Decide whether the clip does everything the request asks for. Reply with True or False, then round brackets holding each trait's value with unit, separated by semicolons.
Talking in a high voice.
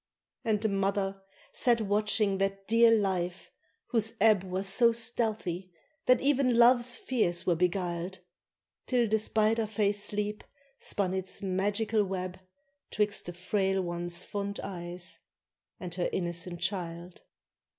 True (195 Hz)